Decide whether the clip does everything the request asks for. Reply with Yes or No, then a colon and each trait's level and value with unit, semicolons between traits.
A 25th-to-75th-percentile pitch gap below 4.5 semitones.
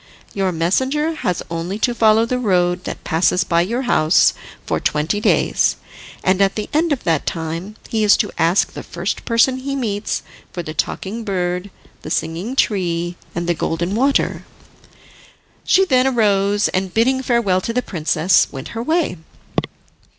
No: wide, 5.4 semitones